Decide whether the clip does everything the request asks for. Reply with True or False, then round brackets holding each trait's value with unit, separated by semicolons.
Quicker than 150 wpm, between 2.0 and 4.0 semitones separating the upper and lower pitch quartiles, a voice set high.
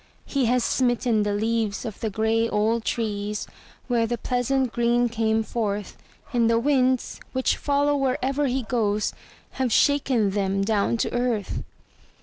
False (145 wpm; 2.8 semitones; 230 Hz)